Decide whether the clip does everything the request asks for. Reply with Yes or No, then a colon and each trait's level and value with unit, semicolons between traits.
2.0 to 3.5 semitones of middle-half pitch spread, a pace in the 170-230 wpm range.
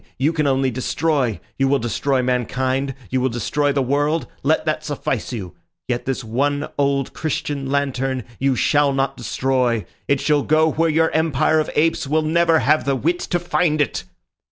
Yes: average, 2.9 semitones; average, 180 wpm